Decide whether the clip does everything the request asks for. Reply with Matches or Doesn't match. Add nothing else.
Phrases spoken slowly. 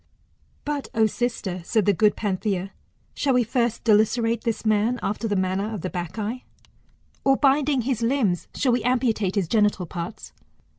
Doesn't match